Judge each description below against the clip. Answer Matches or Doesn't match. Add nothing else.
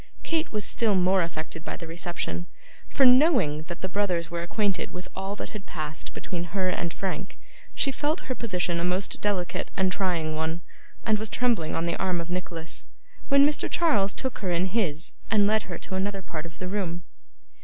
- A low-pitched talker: Doesn't match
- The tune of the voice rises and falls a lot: Doesn't match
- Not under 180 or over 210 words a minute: Matches